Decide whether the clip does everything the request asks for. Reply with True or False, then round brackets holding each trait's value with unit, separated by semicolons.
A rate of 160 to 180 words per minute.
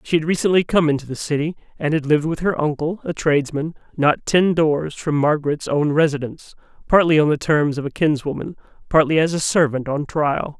False (200 wpm)